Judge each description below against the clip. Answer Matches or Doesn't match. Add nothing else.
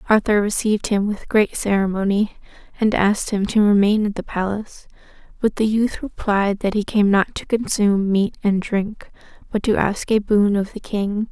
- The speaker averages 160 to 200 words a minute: Matches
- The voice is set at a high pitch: Matches